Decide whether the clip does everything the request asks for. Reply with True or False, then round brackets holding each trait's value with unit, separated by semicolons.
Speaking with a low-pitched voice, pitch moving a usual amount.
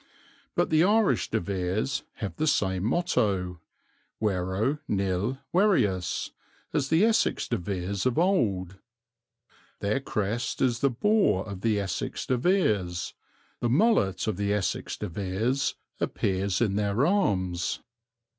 False (105 Hz; 6.3 semitones)